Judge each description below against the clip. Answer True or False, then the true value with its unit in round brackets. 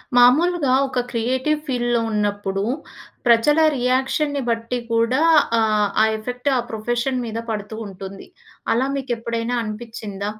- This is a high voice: True (235 Hz)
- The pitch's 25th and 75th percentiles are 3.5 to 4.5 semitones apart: False (2.9 semitones)